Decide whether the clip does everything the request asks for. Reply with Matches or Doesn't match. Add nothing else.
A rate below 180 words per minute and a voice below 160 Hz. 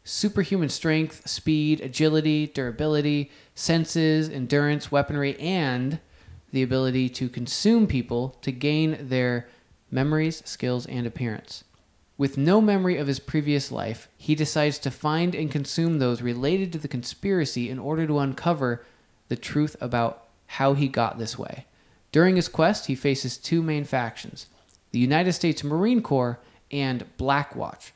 Matches